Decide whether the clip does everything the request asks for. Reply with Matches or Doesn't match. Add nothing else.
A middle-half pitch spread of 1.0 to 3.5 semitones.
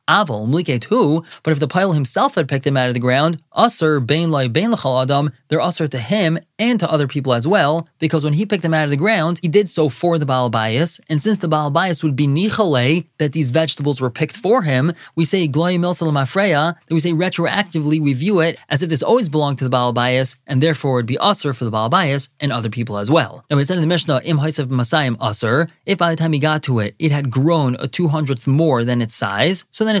Doesn't match